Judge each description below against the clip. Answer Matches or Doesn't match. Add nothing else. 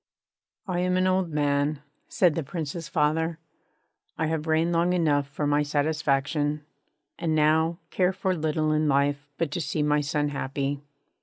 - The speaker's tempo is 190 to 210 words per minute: Doesn't match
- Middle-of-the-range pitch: Matches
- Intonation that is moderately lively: Doesn't match